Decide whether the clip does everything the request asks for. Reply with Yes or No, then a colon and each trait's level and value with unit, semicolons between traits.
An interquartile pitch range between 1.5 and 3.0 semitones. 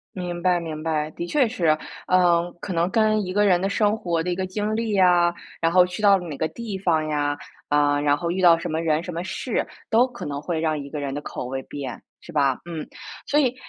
No: average, 3.8 semitones